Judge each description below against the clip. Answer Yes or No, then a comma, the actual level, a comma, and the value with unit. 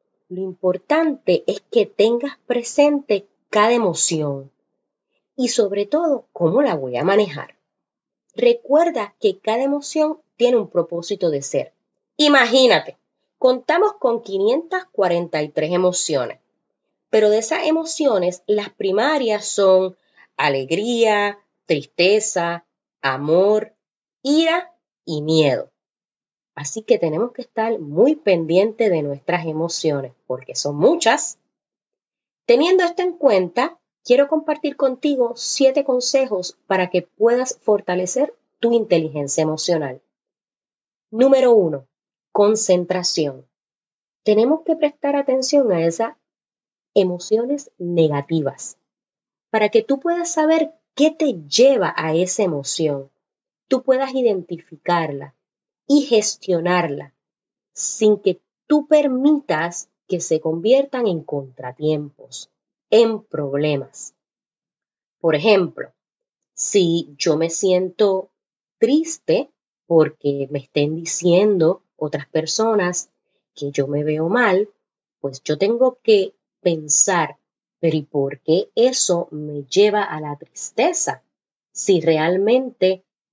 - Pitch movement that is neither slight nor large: No, wide, 8.5 semitones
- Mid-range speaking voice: No, high, 205 Hz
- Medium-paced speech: No, slow, 105 wpm